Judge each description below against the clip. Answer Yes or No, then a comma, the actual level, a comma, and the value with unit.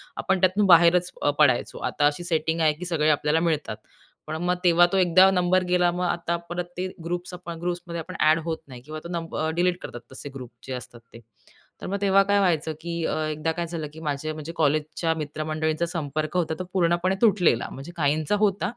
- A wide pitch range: No, narrow, 2.5 semitones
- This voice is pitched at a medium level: Yes, medium, 165 Hz